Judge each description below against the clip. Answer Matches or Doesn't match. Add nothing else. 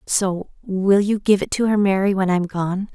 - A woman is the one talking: Matches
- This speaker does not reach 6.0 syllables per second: Matches